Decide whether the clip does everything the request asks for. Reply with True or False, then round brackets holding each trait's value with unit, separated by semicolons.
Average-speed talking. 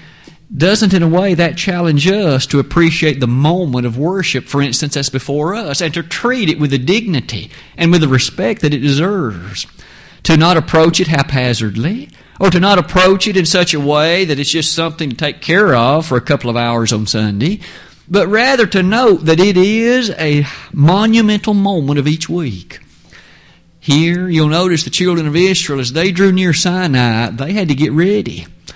True (190 wpm)